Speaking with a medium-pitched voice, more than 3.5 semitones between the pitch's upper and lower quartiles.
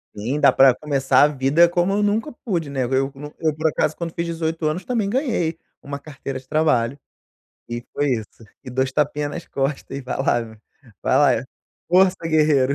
Yes: medium, 150 Hz; average, 4.0 semitones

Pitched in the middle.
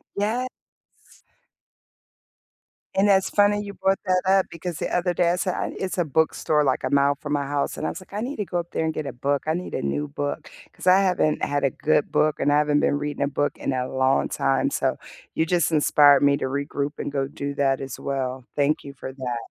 Yes: medium, 145 Hz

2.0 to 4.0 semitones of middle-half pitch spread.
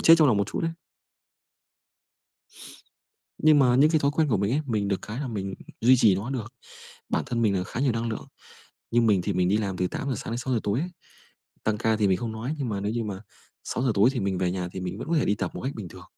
No: average, 4.6 semitones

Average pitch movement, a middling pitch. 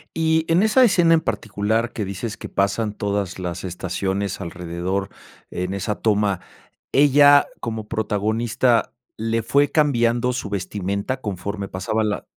No: average, 4.0 semitones; low, 105 Hz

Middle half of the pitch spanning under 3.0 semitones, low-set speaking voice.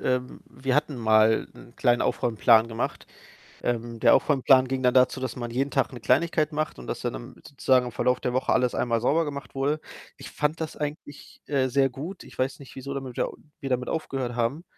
Yes: narrow, 2.6 semitones; low, 130 Hz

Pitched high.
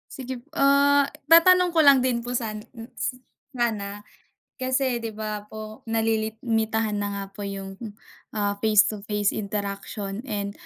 Yes: high, 220 Hz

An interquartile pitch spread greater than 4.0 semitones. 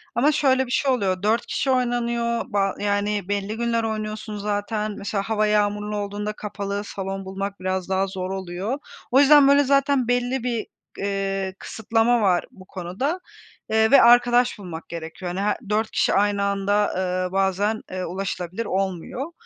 No: average, 3.4 semitones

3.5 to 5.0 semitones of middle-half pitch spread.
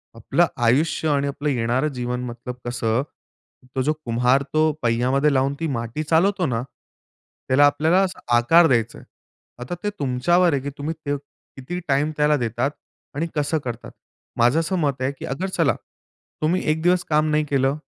Yes: average, 4.0 semitones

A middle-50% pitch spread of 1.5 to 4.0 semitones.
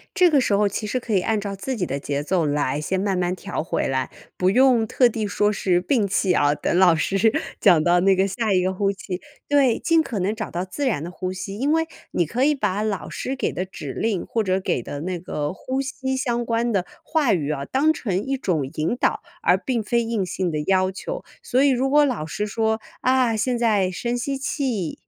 No: average, 5.3 semitones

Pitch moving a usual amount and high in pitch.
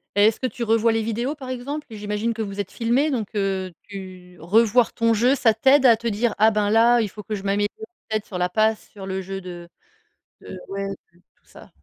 Yes: average, 3.0 semitones; high, 215 Hz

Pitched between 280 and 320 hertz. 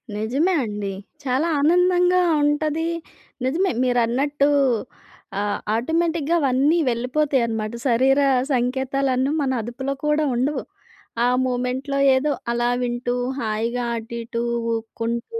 No: very high, 260 Hz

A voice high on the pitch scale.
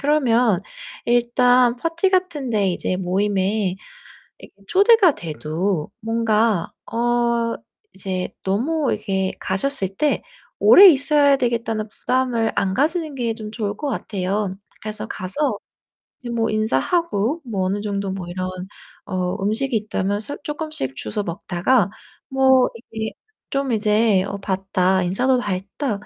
Yes: high, 220 Hz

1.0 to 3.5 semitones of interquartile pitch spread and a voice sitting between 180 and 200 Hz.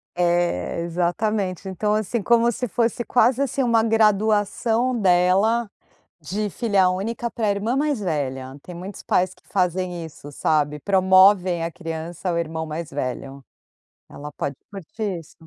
No: average, 4.5 semitones; medium, 185 Hz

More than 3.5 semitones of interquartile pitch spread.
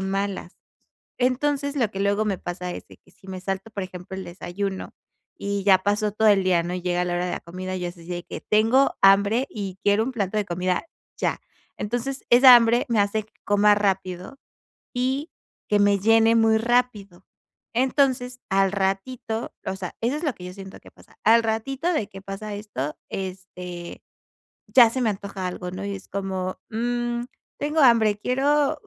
Yes: average, 4.0 semitones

